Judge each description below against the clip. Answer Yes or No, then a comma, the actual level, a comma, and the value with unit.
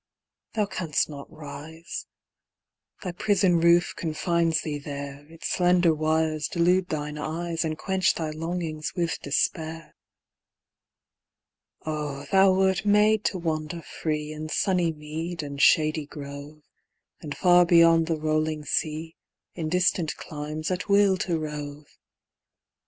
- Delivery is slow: Yes, slow, 125 wpm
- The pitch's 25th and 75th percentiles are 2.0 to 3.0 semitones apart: Yes, narrow, 2.5 semitones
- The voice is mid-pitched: Yes, medium, 160 Hz